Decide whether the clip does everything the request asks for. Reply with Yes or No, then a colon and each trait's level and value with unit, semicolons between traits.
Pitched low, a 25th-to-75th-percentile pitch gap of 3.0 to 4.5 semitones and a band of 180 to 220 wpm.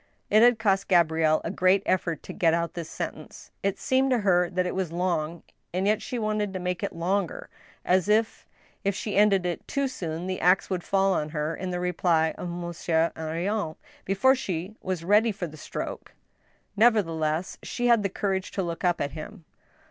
No: medium, 185 Hz; average, 3.3 semitones; average, 195 wpm